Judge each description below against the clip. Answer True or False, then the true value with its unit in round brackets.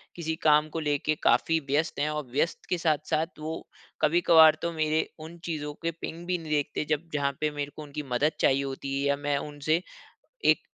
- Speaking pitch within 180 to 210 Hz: False (150 Hz)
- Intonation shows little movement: True (1.8 semitones)